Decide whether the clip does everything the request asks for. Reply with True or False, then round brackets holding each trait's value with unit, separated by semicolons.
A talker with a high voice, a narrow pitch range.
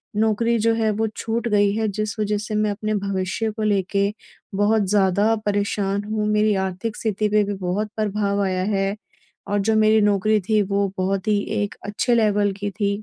True (205 Hz; 1.3 semitones)